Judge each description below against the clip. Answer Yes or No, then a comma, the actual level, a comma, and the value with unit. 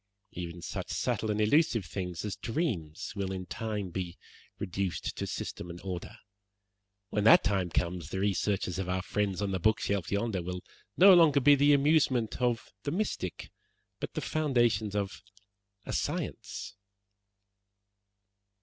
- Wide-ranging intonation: No, average, 4.6 semitones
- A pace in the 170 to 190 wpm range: No, average, 145 wpm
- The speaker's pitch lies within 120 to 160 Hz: No, low, 100 Hz